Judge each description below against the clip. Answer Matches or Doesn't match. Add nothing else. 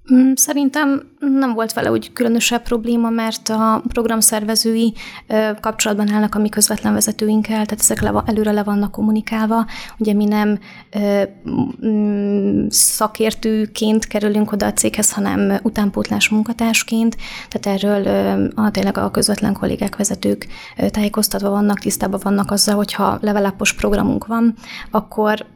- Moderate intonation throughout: Doesn't match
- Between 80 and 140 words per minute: Matches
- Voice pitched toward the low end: Doesn't match